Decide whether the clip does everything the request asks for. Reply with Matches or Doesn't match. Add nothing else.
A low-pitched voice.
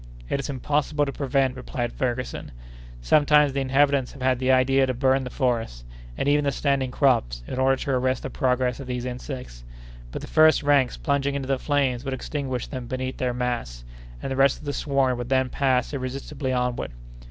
Matches